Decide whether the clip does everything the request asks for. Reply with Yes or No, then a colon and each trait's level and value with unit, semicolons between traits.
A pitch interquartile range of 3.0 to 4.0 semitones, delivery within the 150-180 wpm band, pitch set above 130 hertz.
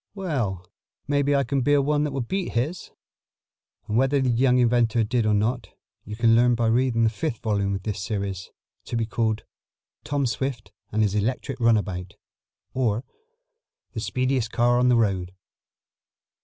No: average, 3.7 semitones; average, 165 wpm; low, 115 Hz